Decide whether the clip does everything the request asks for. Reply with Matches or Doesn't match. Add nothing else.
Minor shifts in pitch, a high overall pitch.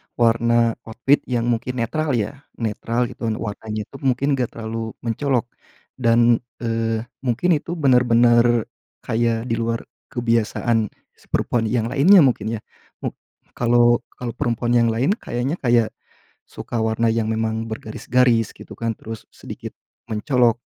Doesn't match